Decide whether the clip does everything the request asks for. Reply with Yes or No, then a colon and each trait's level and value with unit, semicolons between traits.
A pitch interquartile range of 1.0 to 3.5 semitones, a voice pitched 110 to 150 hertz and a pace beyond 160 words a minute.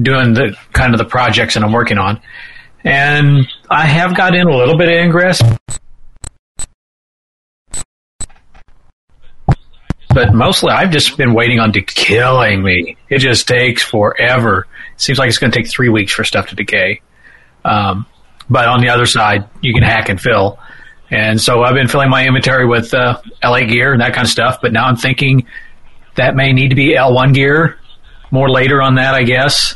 Yes: average, 2.7 semitones; low, 125 Hz; average, 185 wpm